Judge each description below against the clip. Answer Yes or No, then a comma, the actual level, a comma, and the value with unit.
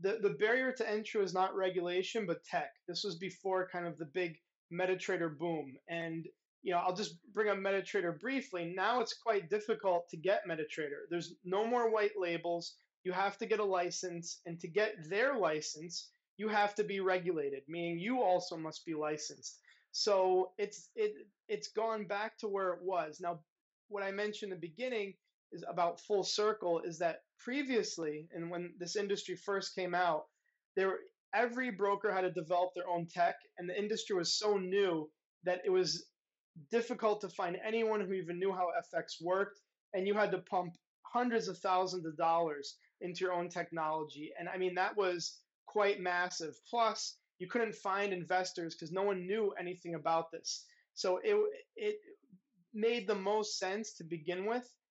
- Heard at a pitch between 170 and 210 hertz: Yes, medium, 185 Hz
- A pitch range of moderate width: Yes, average, 3.5 semitones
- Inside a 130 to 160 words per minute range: No, average, 180 wpm